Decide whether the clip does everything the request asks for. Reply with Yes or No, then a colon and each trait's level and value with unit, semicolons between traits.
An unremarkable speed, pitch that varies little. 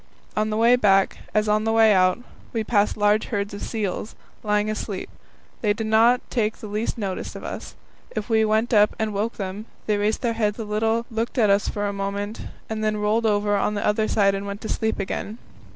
No: fast, 225 wpm; narrow, 1.4 semitones